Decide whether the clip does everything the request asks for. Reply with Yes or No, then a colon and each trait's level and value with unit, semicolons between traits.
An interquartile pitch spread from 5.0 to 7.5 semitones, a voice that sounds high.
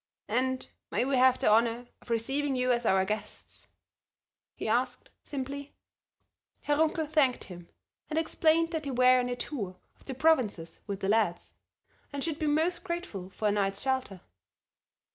Yes: wide, 5.6 semitones; very high, 255 Hz